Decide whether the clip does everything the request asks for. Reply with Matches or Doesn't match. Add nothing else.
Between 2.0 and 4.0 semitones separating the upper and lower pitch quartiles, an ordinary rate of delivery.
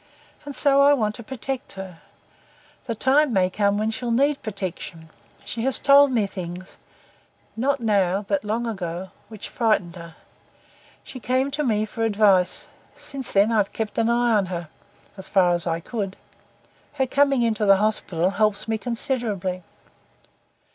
Doesn't match